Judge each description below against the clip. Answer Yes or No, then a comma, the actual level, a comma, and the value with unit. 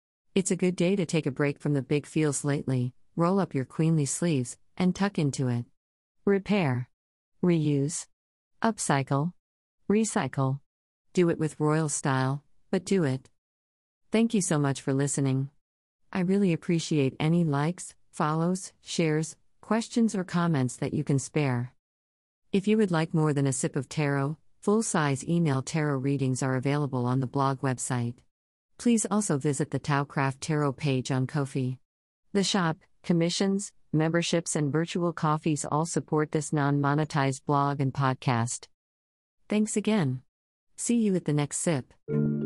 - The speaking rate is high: No, average, 150 wpm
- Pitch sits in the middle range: Yes, medium, 150 Hz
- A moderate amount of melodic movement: Yes, average, 4.5 semitones